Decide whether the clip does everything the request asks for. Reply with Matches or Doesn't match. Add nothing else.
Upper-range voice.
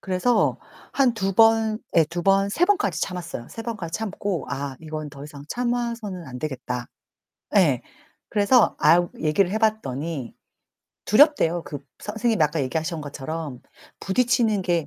Doesn't match